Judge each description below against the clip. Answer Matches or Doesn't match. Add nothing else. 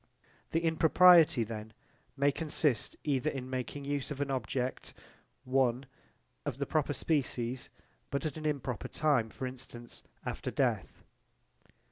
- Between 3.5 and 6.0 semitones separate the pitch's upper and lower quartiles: Doesn't match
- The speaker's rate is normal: Doesn't match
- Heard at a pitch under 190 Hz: Matches